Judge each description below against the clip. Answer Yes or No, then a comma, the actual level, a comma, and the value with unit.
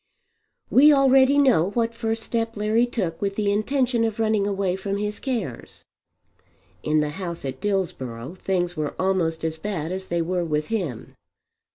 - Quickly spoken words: No, average, 165 wpm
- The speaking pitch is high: Yes, high, 195 Hz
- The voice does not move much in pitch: No, average, 5.2 semitones